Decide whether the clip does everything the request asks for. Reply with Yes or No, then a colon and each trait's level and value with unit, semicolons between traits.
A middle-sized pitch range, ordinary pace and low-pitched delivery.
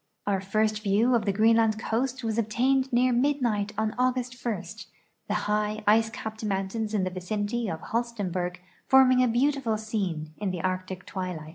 No: average, 3.5 semitones; average, 170 wpm; high, 215 Hz